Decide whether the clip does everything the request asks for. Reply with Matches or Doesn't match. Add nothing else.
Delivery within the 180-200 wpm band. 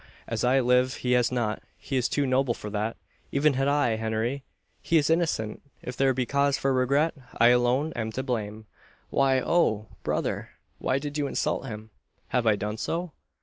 Matches